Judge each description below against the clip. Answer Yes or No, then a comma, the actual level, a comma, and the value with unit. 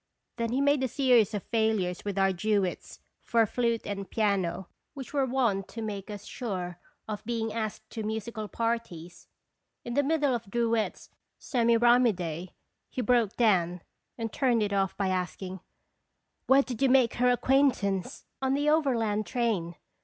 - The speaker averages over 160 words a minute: Yes, average, 170 wpm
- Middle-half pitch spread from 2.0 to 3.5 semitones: No, average, 3.9 semitones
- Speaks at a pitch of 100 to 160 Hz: No, high, 225 Hz